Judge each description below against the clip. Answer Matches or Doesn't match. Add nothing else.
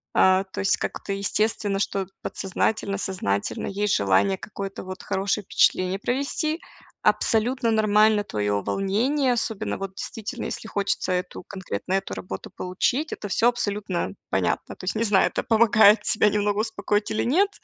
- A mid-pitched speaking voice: Doesn't match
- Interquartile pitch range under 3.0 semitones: Matches